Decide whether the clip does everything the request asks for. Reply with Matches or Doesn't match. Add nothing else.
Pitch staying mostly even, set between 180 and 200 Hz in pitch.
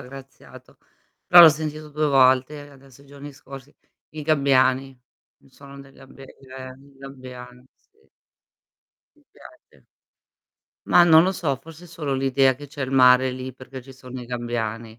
Doesn't match